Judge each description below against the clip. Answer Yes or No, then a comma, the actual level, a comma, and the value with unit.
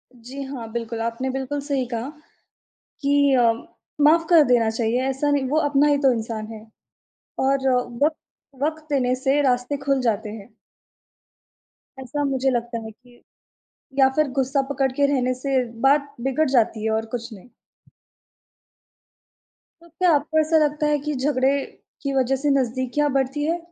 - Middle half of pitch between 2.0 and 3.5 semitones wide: Yes, average, 2.9 semitones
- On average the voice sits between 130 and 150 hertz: No, very high, 265 Hz